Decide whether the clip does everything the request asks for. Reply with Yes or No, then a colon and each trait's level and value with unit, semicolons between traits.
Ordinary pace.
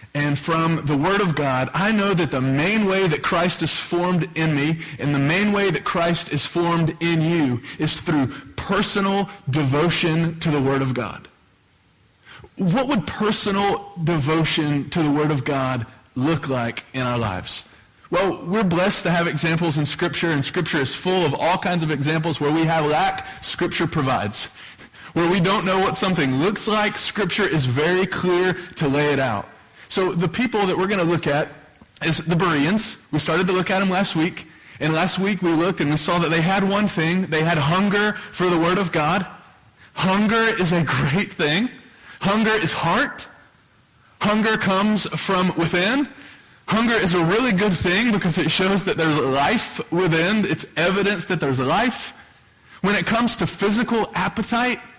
Yes: average, 180 wpm